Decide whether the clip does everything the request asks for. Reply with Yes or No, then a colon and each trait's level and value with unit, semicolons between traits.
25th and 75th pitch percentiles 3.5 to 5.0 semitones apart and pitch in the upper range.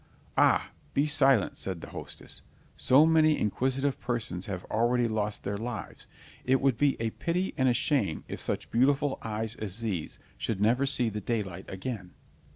No: average, 4.4 semitones; low, 115 Hz